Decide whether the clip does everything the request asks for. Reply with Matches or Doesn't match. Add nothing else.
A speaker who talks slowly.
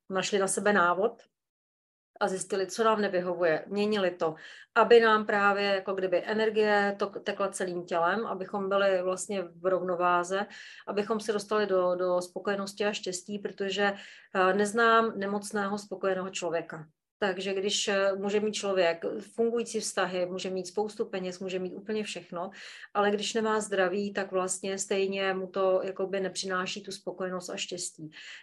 Doesn't match